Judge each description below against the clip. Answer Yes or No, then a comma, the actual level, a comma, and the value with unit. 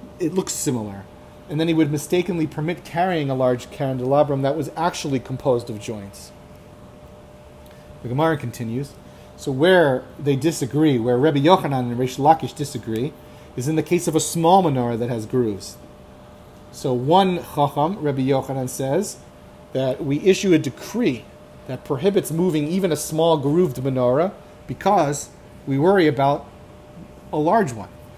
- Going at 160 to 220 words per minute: No, average, 150 wpm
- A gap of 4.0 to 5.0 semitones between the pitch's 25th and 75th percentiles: Yes, average, 4.5 semitones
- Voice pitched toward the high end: No, medium, 140 Hz